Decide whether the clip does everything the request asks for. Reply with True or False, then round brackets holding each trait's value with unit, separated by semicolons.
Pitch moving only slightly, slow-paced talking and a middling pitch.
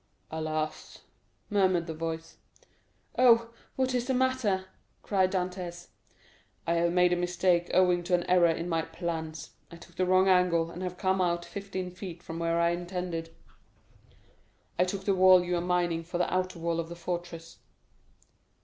False (1.7 semitones; 165 wpm; 175 Hz)